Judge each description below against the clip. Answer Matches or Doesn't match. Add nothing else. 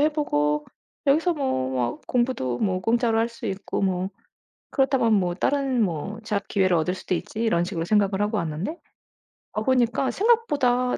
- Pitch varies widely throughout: Matches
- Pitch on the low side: Doesn't match